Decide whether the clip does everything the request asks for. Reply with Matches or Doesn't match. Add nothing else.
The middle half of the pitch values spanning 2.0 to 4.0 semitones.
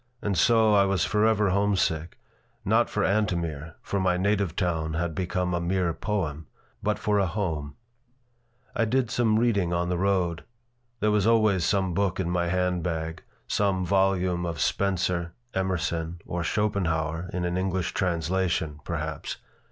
Matches